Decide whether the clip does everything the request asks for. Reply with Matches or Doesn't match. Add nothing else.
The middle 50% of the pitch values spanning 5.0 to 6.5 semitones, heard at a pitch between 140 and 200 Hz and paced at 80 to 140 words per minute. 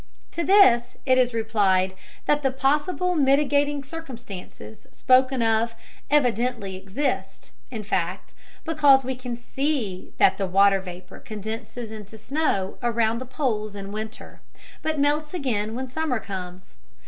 Doesn't match